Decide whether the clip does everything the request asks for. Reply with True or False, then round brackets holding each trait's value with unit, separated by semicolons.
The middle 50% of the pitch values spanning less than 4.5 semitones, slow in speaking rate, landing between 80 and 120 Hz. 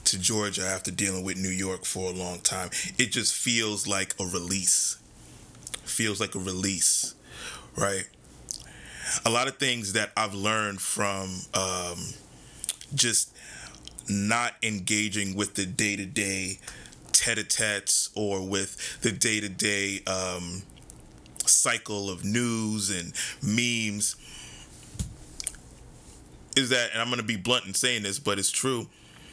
True (3.1 semitones; 130 wpm; 100 Hz)